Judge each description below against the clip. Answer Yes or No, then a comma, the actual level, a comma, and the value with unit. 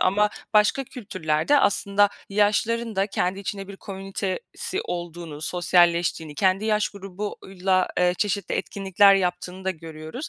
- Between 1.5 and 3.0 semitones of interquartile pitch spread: Yes, narrow, 2.5 semitones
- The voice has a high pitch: Yes, high, 195 Hz